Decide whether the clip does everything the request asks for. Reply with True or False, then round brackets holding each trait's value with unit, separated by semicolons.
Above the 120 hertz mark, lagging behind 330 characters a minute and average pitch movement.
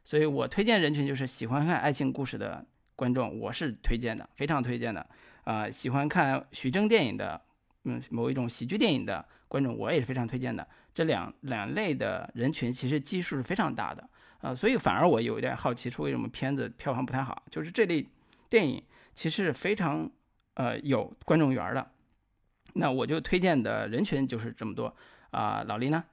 True (135 Hz; 300 characters per minute; 3.6 semitones)